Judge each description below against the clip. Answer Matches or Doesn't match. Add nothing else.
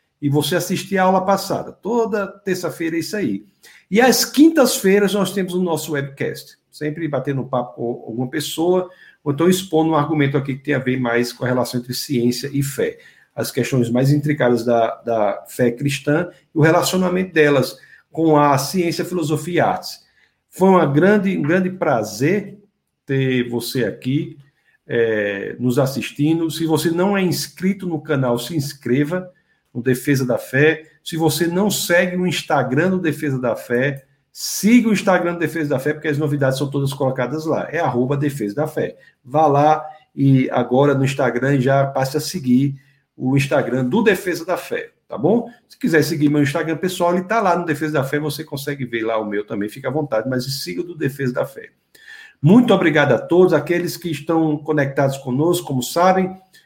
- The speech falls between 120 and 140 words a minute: Doesn't match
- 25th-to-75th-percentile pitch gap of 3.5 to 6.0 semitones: Matches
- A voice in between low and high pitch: Matches